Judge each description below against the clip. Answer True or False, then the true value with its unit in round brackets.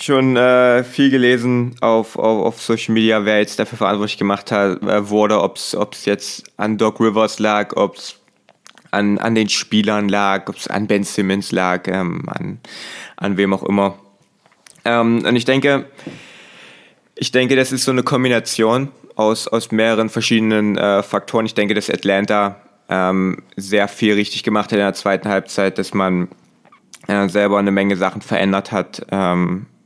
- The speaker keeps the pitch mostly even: True (2.3 semitones)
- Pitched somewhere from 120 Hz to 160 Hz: False (105 Hz)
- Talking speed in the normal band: True (170 wpm)